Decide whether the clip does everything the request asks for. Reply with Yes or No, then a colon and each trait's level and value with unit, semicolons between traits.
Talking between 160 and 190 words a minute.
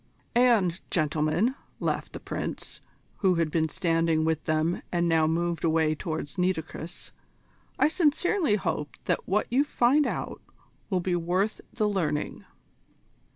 No: slow, 135 wpm